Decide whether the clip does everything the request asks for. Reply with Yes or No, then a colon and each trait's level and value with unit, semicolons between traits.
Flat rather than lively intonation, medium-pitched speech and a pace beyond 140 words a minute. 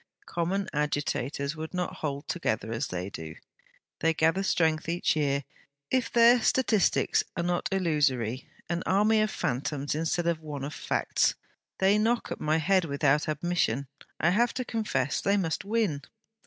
No: average, 5.2 semitones; medium, 160 Hz; average, 160 wpm